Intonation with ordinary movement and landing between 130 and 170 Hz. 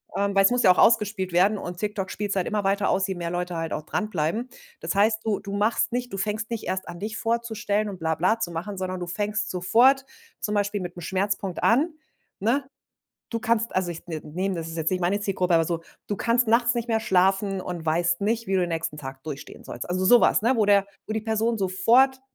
No: average, 3.7 semitones; high, 200 Hz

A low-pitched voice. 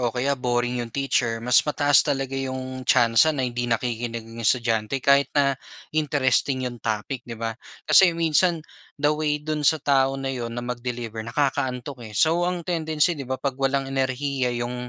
Yes: low, 130 Hz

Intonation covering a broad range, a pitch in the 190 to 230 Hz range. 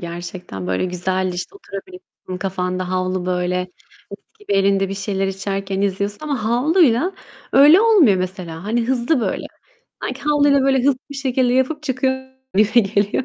Yes: wide, 6.2 semitones; high, 205 Hz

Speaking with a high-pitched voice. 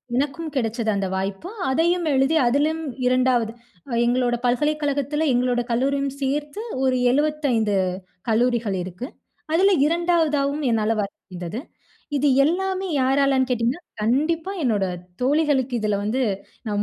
Yes: very high, 265 Hz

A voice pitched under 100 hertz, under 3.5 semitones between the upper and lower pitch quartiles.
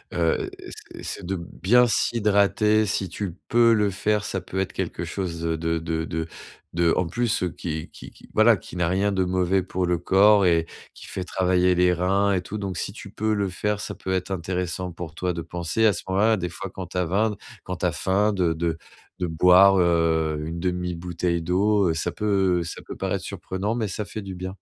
Yes: very low, 90 Hz; average, 2.8 semitones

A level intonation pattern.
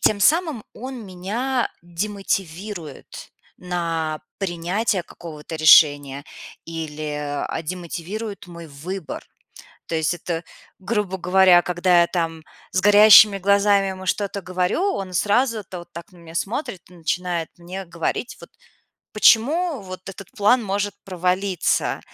No: average, 3.3 semitones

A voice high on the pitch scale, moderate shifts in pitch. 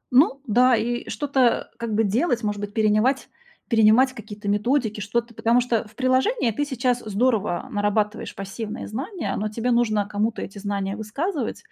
Yes: high, 225 Hz; average, 3.3 semitones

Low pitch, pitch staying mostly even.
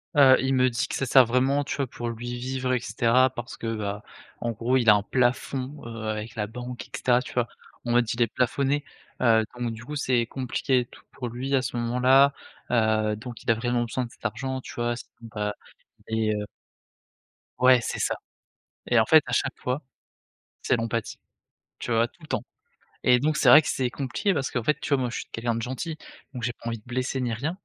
Yes: low, 120 Hz; narrow, 2.1 semitones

